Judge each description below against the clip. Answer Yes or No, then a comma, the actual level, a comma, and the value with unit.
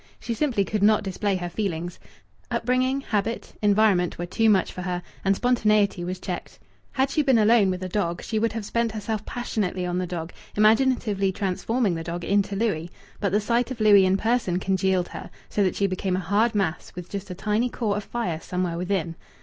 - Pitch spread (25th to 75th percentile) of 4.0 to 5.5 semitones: No, average, 3.5 semitones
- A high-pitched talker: Yes, high, 200 Hz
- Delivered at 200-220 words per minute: Yes, fast, 205 wpm